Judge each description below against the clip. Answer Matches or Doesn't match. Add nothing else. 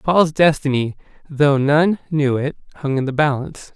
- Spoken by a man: Matches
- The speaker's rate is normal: Matches